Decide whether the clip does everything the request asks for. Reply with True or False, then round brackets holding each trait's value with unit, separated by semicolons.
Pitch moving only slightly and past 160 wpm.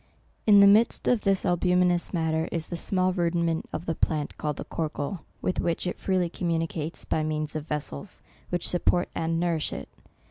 True (2.3 semitones; 180 wpm)